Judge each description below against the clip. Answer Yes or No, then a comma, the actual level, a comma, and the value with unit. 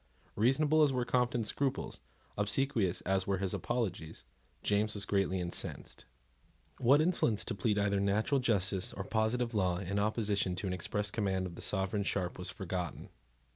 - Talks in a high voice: No, low, 105 Hz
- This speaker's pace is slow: No, average, 160 wpm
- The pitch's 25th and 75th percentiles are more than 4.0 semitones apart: No, average, 3.7 semitones